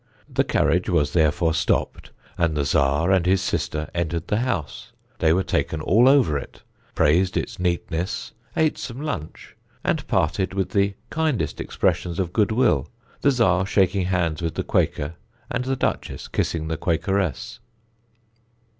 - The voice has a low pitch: Yes, very low, 90 Hz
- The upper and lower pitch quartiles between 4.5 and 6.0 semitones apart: No, average, 3.8 semitones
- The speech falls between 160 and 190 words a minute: No, average, 150 wpm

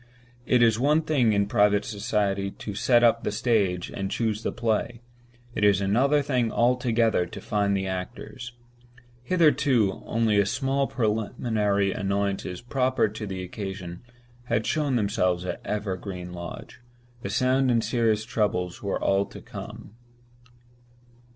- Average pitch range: Yes, average, 3.5 semitones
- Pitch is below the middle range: Yes, low, 110 Hz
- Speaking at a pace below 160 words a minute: Yes, average, 140 wpm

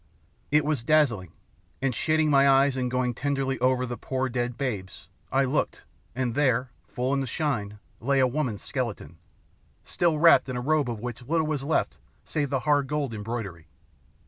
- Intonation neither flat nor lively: Yes, average, 3.0 semitones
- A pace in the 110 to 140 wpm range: No, average, 180 wpm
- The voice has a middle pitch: No, low, 130 Hz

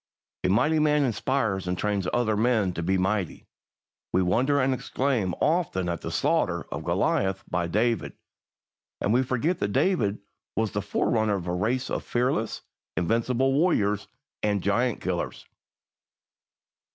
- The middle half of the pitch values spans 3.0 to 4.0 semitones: No, average, 5.1 semitones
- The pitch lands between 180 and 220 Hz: No, low, 110 Hz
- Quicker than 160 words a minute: No, average, 145 wpm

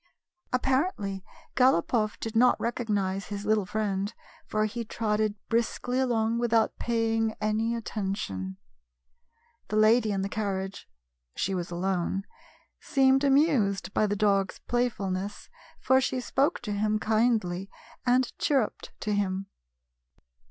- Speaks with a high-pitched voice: Yes, high, 215 Hz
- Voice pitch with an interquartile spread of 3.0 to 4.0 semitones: Yes, average, 3.3 semitones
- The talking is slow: Yes, slow, 130 wpm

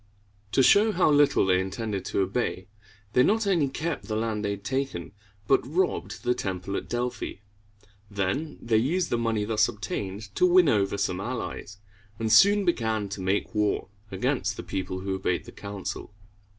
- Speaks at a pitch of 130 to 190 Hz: No, low, 110 Hz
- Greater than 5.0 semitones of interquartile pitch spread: Yes, wide, 5.6 semitones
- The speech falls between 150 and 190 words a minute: Yes, average, 175 wpm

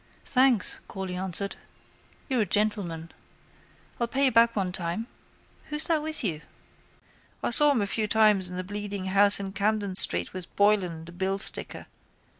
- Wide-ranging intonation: No, average, 3.5 semitones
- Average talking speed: Yes, average, 160 wpm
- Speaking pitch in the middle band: No, high, 200 Hz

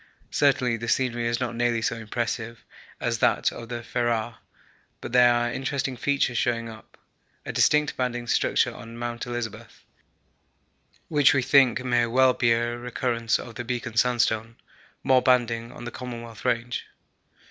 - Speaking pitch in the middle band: No, low, 120 Hz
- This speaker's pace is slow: No, average, 155 wpm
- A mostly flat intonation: Yes, narrow, 1.3 semitones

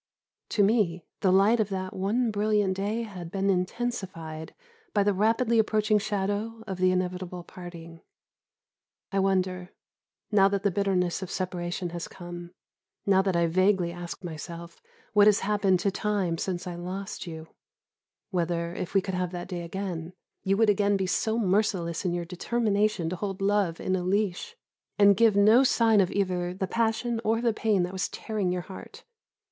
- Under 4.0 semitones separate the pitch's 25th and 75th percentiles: Yes, average, 2.7 semitones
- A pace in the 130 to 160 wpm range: No, average, 170 wpm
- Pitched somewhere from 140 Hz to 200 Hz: Yes, high, 190 Hz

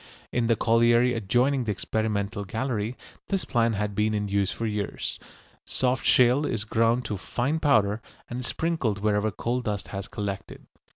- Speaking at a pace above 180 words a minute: No, average, 165 wpm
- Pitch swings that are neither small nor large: Yes, average, 3.1 semitones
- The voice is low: Yes, low, 115 Hz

